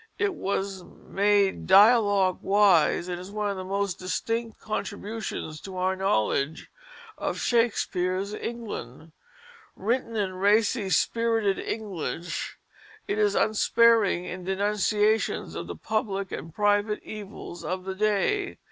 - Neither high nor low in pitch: No, high, 200 Hz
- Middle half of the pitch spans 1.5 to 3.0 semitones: Yes, narrow, 2.5 semitones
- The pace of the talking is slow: Yes, slow, 120 wpm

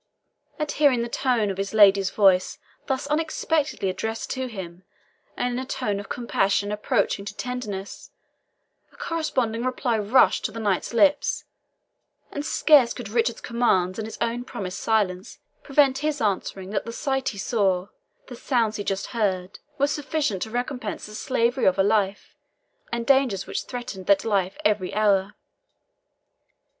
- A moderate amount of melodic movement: Yes, average, 4.5 semitones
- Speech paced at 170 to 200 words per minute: No, average, 155 wpm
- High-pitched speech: Yes, high, 225 Hz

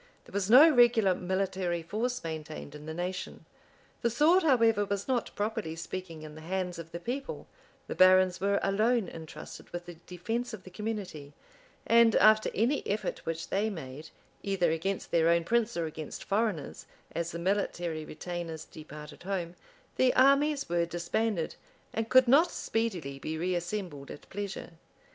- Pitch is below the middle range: No, medium, 185 Hz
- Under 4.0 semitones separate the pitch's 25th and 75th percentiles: No, average, 5.2 semitones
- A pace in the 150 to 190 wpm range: Yes, average, 160 wpm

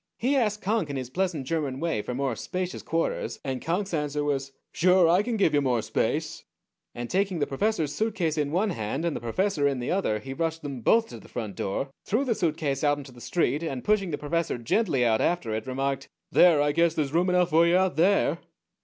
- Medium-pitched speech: Yes, medium, 155 Hz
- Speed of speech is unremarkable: No, fast, 225 wpm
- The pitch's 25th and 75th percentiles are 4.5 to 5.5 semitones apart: Yes, average, 5.2 semitones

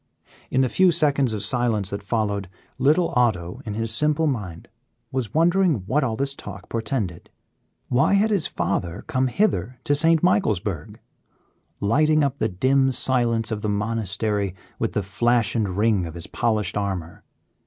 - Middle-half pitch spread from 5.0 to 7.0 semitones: Yes, wide, 5.4 semitones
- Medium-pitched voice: No, low, 115 Hz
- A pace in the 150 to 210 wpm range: Yes, average, 160 wpm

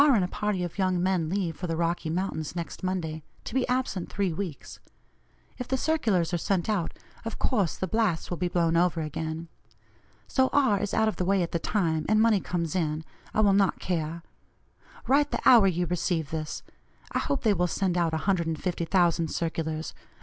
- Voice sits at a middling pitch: Yes, medium, 180 Hz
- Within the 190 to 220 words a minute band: Yes, average, 195 wpm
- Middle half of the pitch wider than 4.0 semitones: No, average, 3.7 semitones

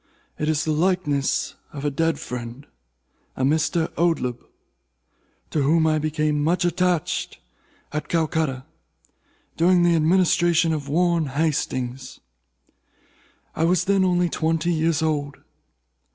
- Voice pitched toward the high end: No, medium, 155 Hz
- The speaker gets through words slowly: Yes, slow, 110 wpm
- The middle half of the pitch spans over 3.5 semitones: No, average, 3.0 semitones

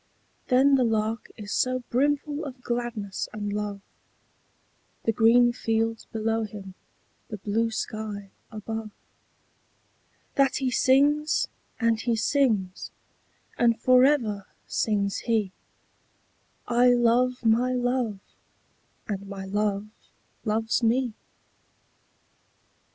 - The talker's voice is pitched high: Yes, high, 225 Hz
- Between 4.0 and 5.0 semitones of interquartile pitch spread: No, average, 2.9 semitones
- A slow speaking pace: Yes, slow, 100 wpm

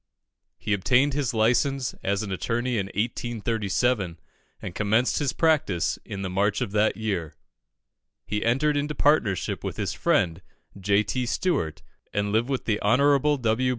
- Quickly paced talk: No, average, 150 wpm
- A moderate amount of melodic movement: Yes, average, 4.4 semitones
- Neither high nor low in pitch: No, low, 110 Hz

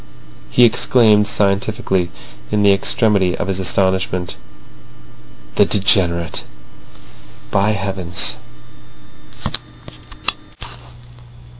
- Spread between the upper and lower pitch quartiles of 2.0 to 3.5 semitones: Yes, narrow, 2.6 semitones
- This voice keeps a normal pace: No, slow, 60 wpm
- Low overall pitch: Yes, very low, 95 Hz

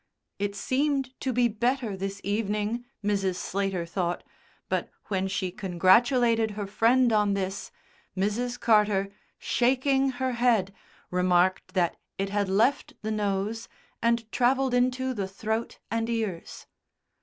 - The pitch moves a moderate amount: Yes, average, 3.8 semitones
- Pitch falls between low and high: No, high, 215 Hz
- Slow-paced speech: Yes, slow, 130 wpm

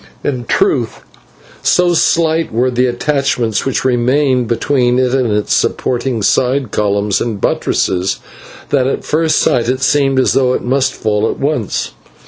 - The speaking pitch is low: Yes, low, 125 Hz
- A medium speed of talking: Yes, average, 150 wpm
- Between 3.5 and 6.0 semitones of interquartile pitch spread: No, average, 2.9 semitones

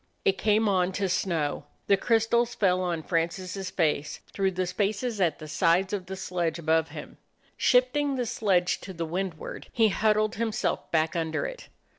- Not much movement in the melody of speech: No, average, 4.1 semitones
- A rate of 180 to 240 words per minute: No, average, 170 wpm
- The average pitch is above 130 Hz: Yes, high, 190 Hz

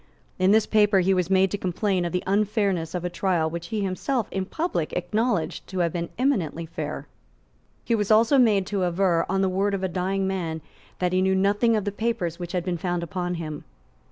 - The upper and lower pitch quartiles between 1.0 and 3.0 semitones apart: Yes, average, 2.7 semitones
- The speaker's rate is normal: No, fast, 220 wpm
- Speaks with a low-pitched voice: No, high, 190 Hz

